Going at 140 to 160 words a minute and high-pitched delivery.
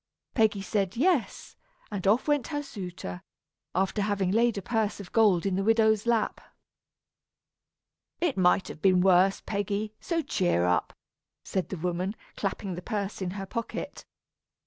Yes: average, 150 wpm; high, 200 Hz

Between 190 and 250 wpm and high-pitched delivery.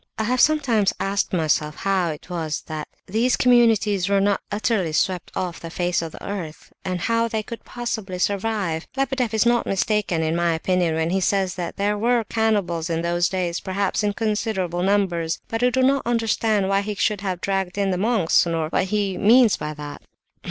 Yes: average, 195 wpm; high, 195 Hz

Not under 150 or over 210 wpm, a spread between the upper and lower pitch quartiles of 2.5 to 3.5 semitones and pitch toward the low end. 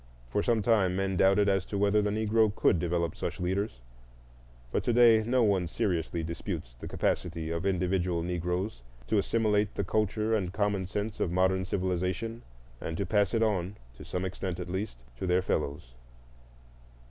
Yes: average, 170 wpm; average, 3.0 semitones; very low, 95 Hz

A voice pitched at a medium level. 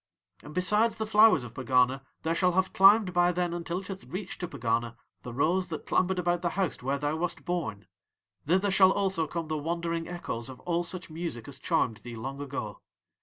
Yes: medium, 170 Hz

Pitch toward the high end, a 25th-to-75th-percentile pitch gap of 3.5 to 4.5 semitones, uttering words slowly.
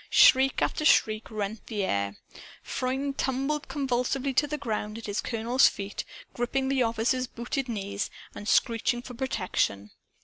No: high, 240 Hz; average, 3.9 semitones; average, 145 wpm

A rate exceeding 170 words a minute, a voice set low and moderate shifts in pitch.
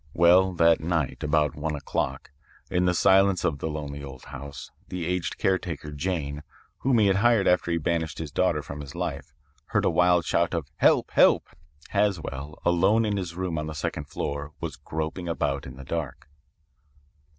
Yes: average, 180 wpm; very low, 80 Hz; average, 3.7 semitones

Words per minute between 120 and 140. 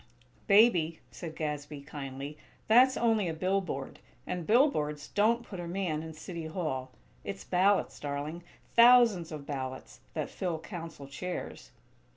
Yes: slow, 135 wpm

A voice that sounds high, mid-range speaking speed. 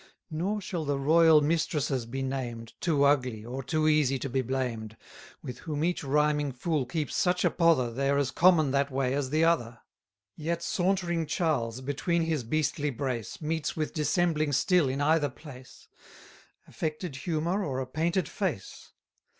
No: medium, 150 Hz; average, 165 wpm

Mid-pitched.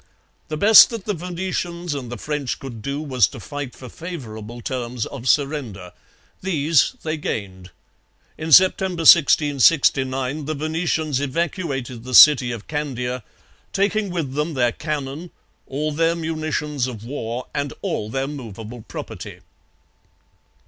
Yes: medium, 145 Hz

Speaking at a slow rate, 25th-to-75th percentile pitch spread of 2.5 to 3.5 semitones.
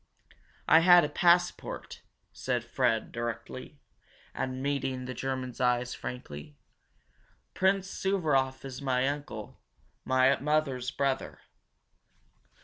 Yes: slow, 100 wpm; average, 2.9 semitones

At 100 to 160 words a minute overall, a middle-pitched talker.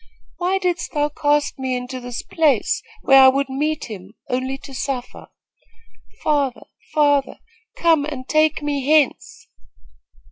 No: slow, 135 wpm; very high, 280 Hz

